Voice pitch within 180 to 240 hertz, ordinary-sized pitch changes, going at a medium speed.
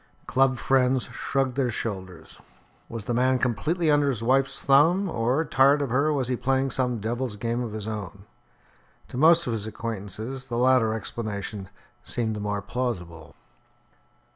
No: low, 125 Hz; average, 3.6 semitones; average, 160 wpm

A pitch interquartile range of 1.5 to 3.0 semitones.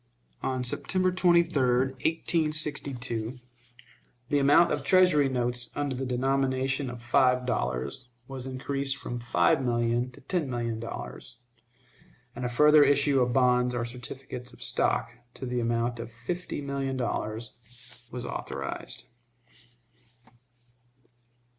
Yes: narrow, 2.6 semitones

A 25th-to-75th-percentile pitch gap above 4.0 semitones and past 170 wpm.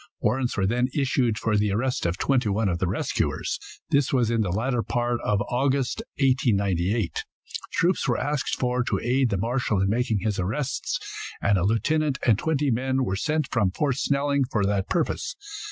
Yes: average, 4.6 semitones; average, 185 wpm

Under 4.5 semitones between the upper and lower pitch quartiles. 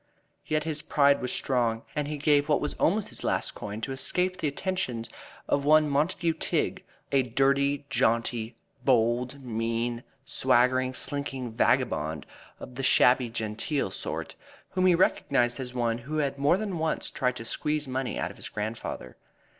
Yes: average, 3.9 semitones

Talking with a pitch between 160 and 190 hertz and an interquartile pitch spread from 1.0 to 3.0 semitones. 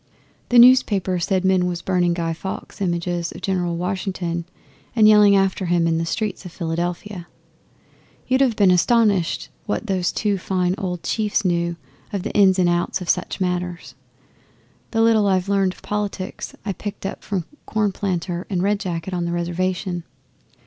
Yes: medium, 185 Hz; narrow, 2.6 semitones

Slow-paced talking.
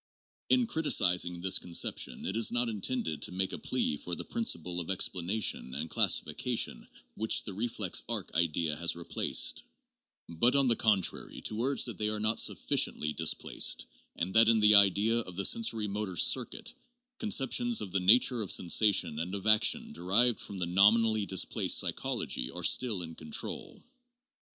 No: average, 165 wpm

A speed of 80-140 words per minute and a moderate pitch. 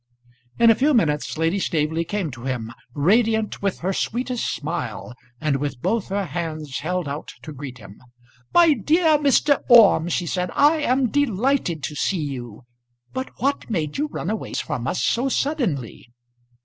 No: average, 165 wpm; medium, 180 Hz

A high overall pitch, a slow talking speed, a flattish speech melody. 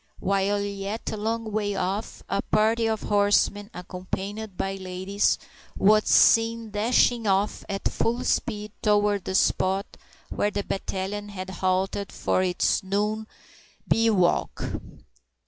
Yes: high, 205 Hz; slow, 125 wpm; narrow, 1.9 semitones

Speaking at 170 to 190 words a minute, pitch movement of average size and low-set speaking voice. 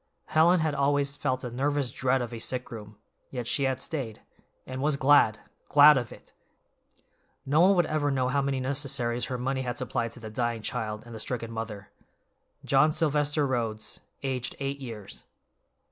Yes: average, 175 wpm; average, 3.3 semitones; low, 130 Hz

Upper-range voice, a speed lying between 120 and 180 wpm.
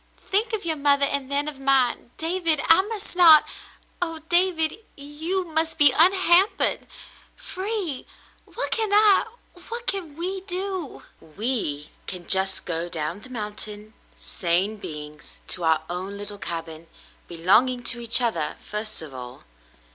Yes: very high, 280 Hz; average, 150 wpm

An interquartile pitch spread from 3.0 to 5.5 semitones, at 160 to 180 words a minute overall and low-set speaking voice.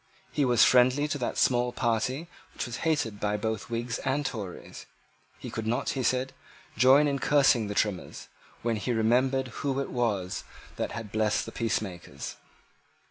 Yes: average, 3.3 semitones; average, 165 wpm; low, 120 Hz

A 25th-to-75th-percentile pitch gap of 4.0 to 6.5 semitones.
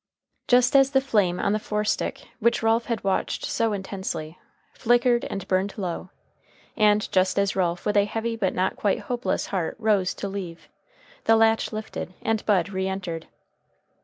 No: average, 3.0 semitones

